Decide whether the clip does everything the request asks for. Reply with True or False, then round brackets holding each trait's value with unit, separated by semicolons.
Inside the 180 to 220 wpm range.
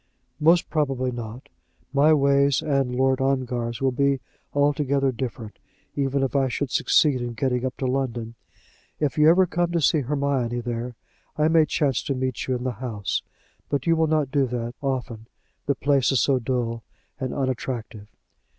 False (170 wpm)